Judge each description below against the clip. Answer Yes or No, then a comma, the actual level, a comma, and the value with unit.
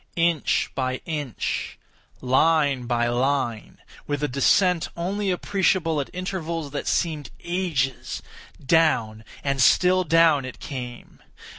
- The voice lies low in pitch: No, medium, 150 Hz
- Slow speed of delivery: Yes, slow, 100 wpm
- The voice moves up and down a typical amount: Yes, average, 4.6 semitones